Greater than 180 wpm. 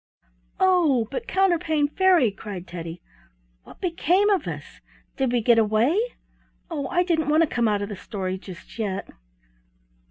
No: average, 155 wpm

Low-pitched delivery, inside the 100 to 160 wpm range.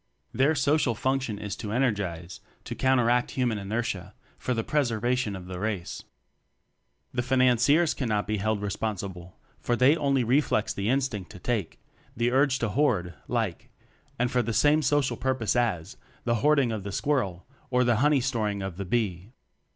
No: low, 120 Hz; average, 175 wpm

